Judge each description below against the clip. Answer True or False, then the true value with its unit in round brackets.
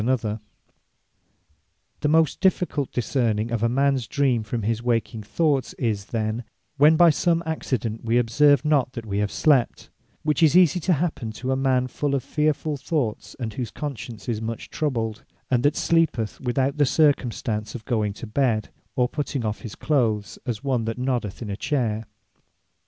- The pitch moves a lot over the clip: False (4.4 semitones)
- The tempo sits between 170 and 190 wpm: True (180 wpm)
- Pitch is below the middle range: True (125 Hz)